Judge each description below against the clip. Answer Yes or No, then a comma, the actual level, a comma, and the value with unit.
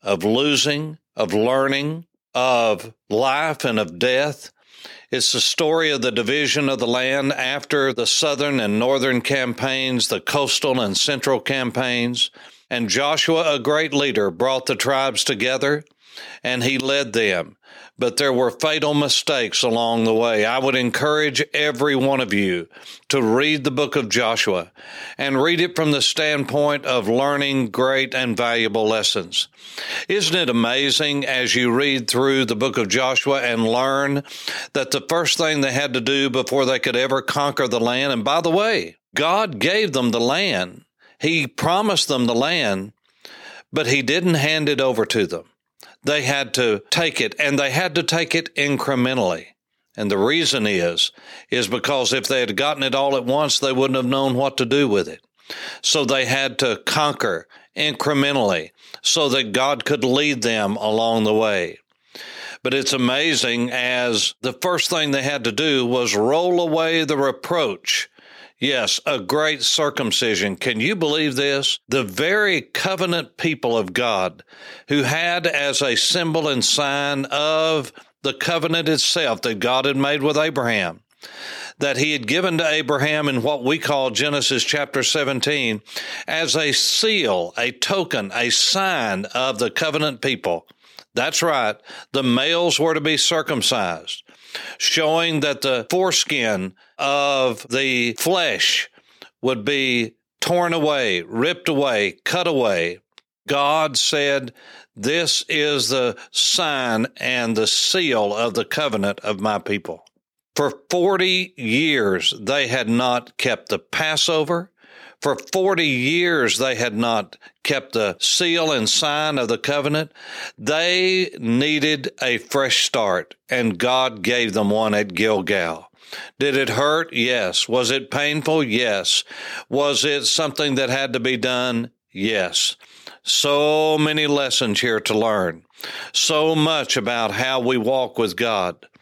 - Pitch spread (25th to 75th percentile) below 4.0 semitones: Yes, average, 3.5 semitones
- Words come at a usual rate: Yes, average, 150 wpm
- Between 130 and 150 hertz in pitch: Yes, low, 135 Hz